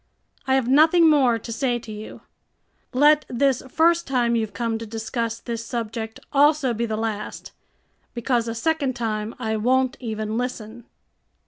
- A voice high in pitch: Yes, high, 235 Hz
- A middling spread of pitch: Yes, average, 3.0 semitones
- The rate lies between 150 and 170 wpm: Yes, average, 155 wpm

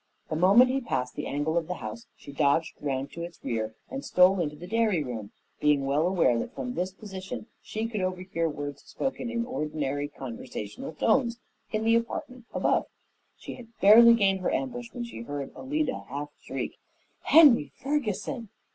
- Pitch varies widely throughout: Yes, wide, 8.3 semitones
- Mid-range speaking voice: Yes, medium, 180 Hz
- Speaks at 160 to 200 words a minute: Yes, average, 175 wpm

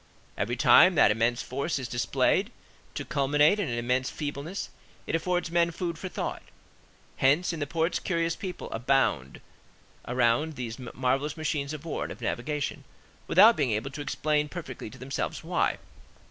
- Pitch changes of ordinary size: Yes, average, 4.4 semitones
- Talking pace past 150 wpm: Yes, average, 160 wpm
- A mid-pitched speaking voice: Yes, medium, 145 Hz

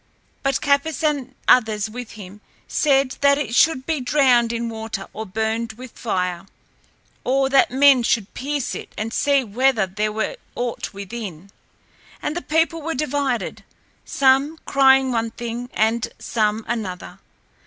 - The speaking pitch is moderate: No, high, 245 Hz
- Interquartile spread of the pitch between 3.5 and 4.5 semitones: Yes, average, 3.9 semitones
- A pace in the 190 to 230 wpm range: No, average, 145 wpm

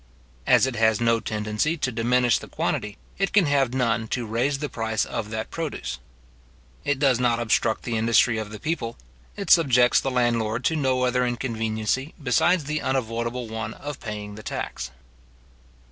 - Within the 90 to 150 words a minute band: No, average, 170 wpm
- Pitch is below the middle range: Yes, low, 120 Hz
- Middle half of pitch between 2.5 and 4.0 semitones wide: Yes, average, 3.2 semitones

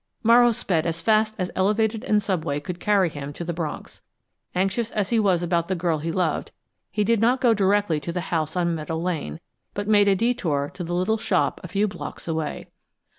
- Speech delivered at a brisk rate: Yes, fast, 210 wpm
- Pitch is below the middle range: No, medium, 185 Hz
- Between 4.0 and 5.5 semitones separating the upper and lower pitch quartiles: Yes, average, 4.3 semitones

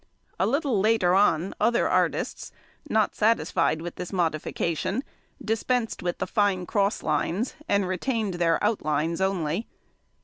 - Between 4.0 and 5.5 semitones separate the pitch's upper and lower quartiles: Yes, average, 4.4 semitones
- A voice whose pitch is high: Yes, high, 195 Hz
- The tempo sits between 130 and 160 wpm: Yes, slow, 135 wpm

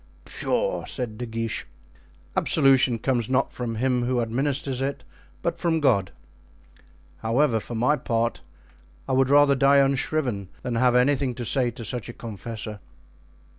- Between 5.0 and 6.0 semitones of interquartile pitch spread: No, average, 2.9 semitones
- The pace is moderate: Yes, average, 145 wpm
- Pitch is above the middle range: No, low, 125 Hz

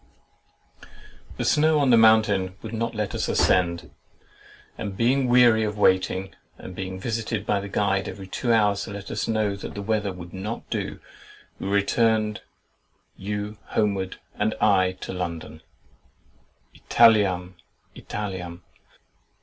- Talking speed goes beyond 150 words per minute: No, average, 140 wpm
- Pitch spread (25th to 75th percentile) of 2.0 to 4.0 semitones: Yes, average, 2.8 semitones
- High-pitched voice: No, low, 105 Hz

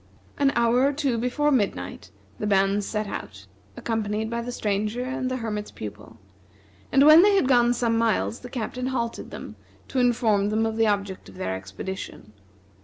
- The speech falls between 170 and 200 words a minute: Yes, average, 180 wpm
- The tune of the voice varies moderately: Yes, average, 3.6 semitones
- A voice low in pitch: No, high, 230 Hz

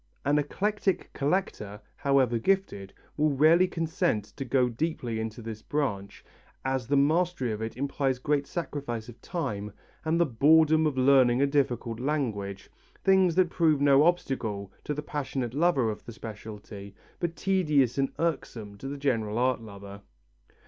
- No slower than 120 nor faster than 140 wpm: No, average, 155 wpm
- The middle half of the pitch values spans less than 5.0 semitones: No, wide, 5.6 semitones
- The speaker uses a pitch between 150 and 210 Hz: No, low, 135 Hz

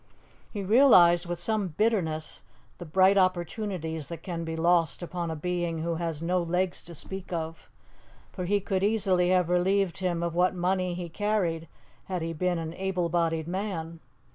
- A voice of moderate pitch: Yes, medium, 175 Hz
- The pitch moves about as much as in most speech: No, narrow, 2.3 semitones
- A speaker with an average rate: Yes, average, 170 wpm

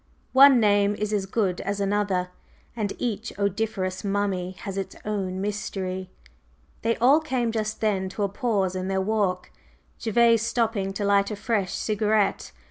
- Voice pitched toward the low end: No, high, 205 Hz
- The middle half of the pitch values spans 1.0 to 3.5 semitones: Yes, narrow, 2.4 semitones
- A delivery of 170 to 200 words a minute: No, average, 155 wpm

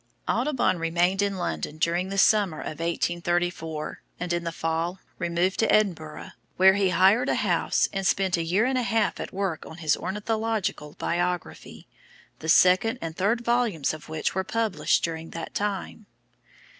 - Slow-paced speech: No, average, 165 wpm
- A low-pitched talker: No, medium, 180 Hz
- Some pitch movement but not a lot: Yes, average, 3.5 semitones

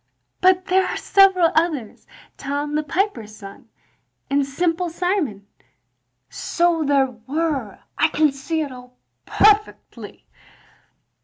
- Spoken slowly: Yes, slow, 110 wpm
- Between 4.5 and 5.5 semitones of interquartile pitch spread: Yes, average, 4.8 semitones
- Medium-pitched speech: No, very high, 310 Hz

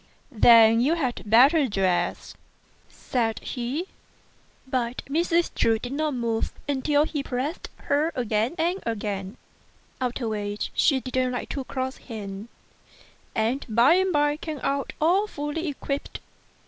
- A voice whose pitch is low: No, very high, 260 Hz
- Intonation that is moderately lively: Yes, average, 4.5 semitones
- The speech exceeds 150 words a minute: No, slow, 135 wpm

